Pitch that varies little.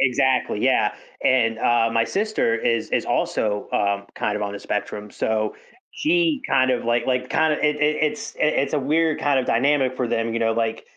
No: average, 4.8 semitones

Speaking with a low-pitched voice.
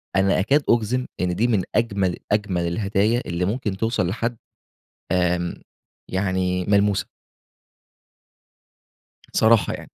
Yes: low, 100 Hz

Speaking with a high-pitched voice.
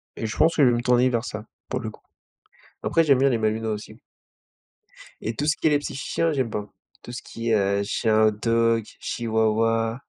No: low, 115 Hz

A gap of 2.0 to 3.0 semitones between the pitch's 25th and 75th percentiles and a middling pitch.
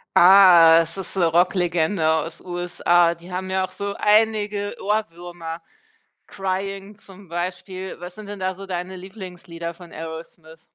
Yes: narrow, 2.4 semitones; medium, 180 Hz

